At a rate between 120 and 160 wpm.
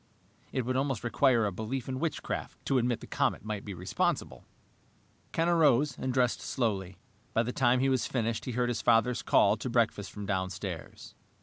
No: average, 185 wpm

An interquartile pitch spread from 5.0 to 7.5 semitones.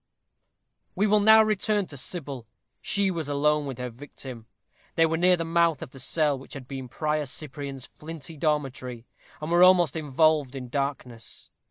No: average, 3.9 semitones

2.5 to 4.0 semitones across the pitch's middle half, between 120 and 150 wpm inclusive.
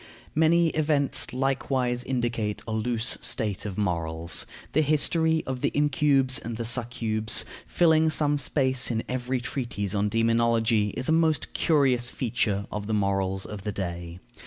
No: average, 4.8 semitones; average, 145 wpm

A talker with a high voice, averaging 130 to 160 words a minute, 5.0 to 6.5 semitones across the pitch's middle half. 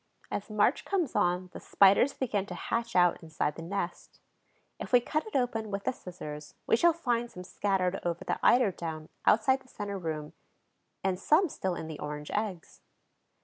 No: high, 200 Hz; average, 185 wpm; wide, 5.5 semitones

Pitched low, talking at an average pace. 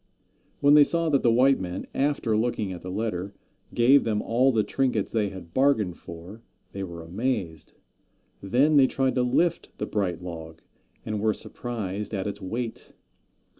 Yes: low, 110 Hz; average, 170 wpm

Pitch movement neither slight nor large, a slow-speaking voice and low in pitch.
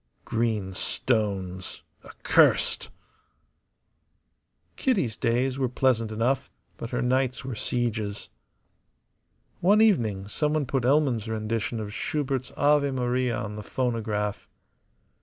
Yes: average, 3.5 semitones; slow, 100 wpm; low, 120 Hz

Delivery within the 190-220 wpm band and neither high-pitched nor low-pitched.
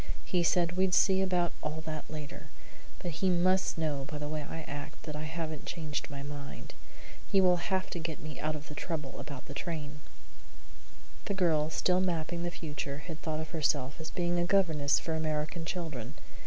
Yes: average, 195 wpm; medium, 160 Hz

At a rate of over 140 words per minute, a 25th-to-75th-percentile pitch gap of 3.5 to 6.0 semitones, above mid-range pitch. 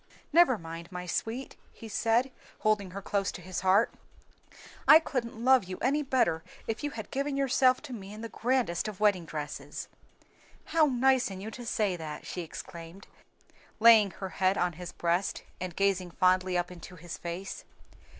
Yes: average, 175 wpm; average, 5.3 semitones; high, 200 Hz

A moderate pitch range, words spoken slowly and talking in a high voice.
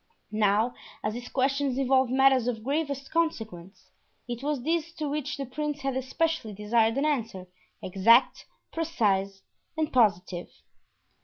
Yes: average, 4.7 semitones; slow, 130 wpm; very high, 255 Hz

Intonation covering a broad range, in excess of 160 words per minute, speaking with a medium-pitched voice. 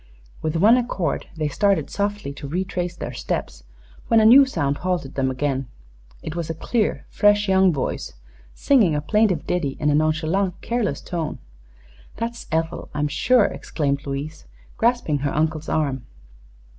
No: wide, 5.8 semitones; average, 155 wpm; medium, 160 Hz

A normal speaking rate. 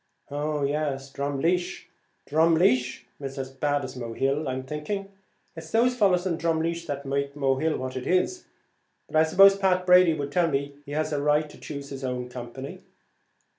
Yes: average, 170 wpm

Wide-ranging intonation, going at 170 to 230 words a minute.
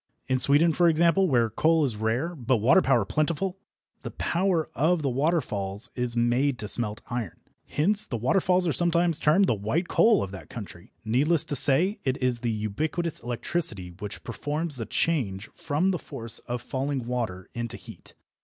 Yes: wide, 6.4 semitones; average, 175 wpm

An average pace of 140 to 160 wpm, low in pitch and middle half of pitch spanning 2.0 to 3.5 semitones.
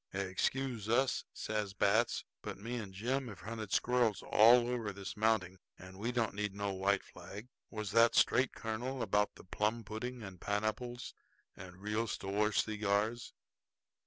Yes: average, 155 wpm; low, 110 Hz; average, 2.8 semitones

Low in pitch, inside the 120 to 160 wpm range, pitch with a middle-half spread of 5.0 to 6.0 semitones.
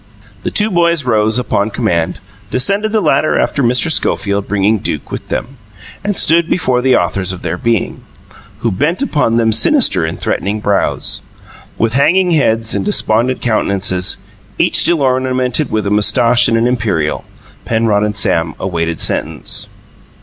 Yes: low, 115 Hz; average, 155 wpm; wide, 5.5 semitones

